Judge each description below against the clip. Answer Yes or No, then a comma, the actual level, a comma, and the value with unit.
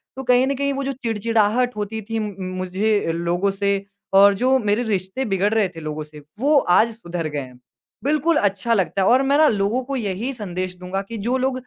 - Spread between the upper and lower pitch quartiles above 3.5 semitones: Yes, average, 4.8 semitones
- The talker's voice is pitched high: Yes, high, 210 Hz